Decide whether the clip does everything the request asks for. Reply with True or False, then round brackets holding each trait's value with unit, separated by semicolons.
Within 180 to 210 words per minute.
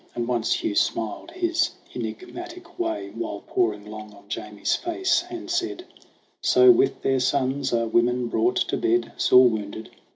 False (155 wpm)